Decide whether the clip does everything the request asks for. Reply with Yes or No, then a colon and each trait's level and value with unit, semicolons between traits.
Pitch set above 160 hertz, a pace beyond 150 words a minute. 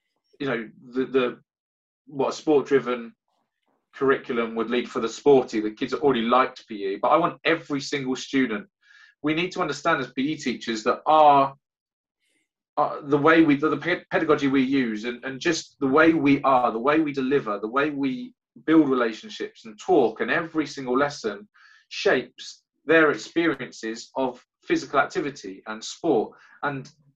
No: medium, 140 Hz; average, 165 wpm